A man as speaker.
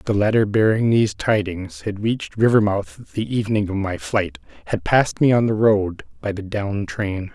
Yes: male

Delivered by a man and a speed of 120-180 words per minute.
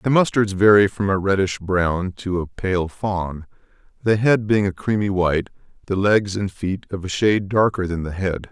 No: male; average, 195 wpm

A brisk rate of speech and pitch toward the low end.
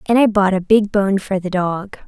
No: fast, 260 wpm; high, 195 Hz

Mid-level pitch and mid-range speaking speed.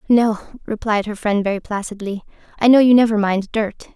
No: high, 215 Hz; average, 180 wpm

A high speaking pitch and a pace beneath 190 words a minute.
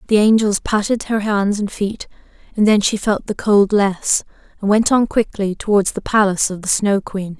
No: high, 205 Hz; fast, 205 wpm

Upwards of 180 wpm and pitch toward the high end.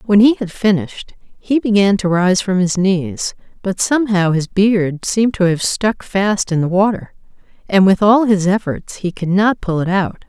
Yes: average, 200 wpm; high, 195 Hz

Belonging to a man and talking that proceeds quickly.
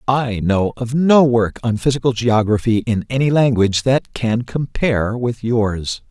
No: male; average, 155 wpm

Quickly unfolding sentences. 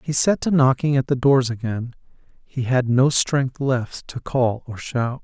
No: average, 195 wpm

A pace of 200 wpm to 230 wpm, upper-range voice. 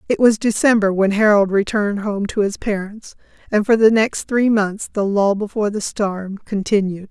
No: average, 185 wpm; high, 210 Hz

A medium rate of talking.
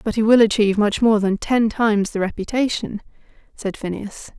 Yes: average, 180 wpm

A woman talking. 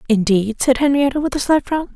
Yes: female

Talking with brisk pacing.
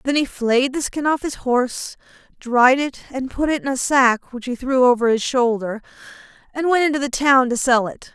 Yes: fast, 220 wpm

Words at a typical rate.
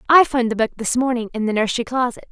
No: fast, 260 wpm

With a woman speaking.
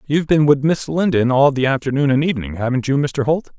No: male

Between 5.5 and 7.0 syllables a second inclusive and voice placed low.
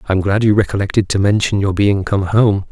Yes: 6.0 syllables/s; low, 100 Hz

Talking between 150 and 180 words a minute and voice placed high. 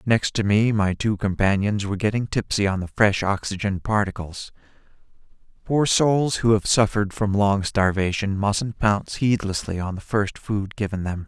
No: average, 165 wpm; low, 100 Hz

